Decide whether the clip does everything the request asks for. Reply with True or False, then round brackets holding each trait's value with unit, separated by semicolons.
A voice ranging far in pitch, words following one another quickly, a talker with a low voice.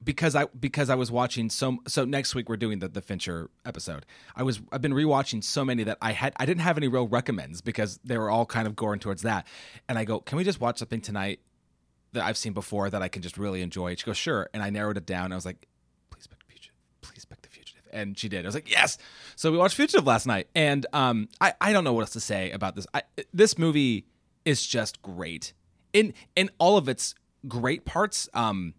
True (5.8 semitones; 250 wpm; 115 Hz)